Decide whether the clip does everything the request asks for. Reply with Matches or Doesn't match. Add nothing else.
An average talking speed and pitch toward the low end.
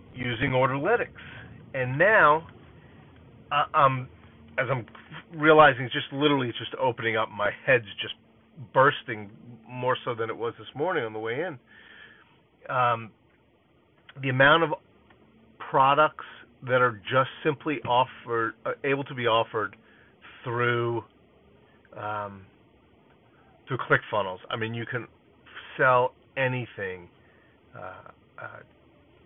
Doesn't match